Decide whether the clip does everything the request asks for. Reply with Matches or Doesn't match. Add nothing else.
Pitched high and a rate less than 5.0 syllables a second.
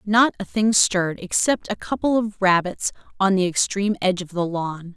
Doesn't match